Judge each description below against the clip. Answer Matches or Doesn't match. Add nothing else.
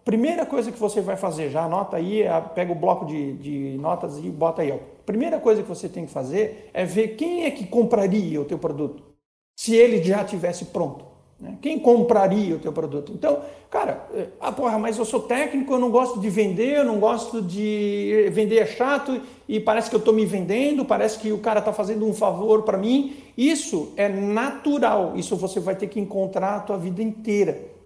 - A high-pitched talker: Matches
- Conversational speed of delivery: Doesn't match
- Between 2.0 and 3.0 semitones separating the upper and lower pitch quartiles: Doesn't match